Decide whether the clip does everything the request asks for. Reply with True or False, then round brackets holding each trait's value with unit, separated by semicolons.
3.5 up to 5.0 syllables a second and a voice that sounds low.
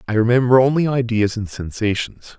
False (5.4 syllables/s; 115 Hz)